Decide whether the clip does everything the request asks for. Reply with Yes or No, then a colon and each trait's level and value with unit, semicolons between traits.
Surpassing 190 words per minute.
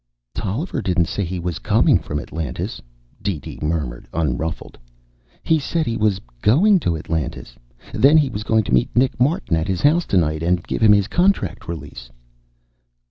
No: average, 165 wpm